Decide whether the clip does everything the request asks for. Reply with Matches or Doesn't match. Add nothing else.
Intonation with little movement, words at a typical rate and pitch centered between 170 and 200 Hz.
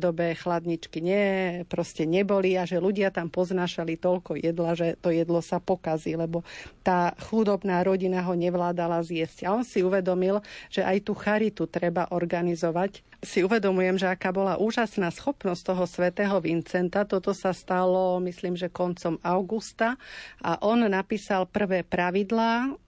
Matches